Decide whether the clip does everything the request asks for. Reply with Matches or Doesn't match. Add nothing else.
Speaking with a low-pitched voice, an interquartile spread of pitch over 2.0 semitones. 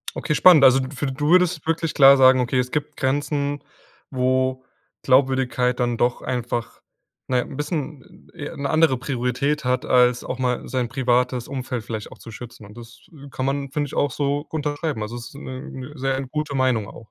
Matches